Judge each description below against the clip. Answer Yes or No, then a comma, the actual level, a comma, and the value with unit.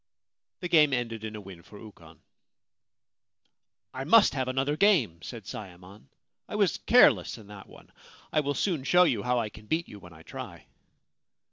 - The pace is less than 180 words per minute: No, average, 190 wpm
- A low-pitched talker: Yes, low, 115 Hz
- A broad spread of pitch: Yes, wide, 6.6 semitones